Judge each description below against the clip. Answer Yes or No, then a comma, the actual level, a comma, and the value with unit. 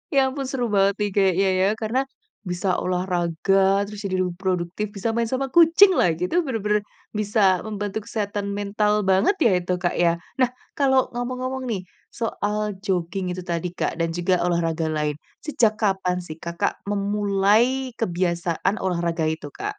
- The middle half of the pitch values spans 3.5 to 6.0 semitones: Yes, average, 3.9 semitones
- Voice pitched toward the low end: No, high, 200 Hz